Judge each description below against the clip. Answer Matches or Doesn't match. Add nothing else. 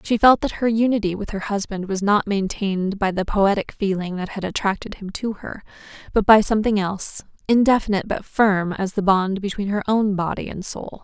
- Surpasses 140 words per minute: Matches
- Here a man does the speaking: Doesn't match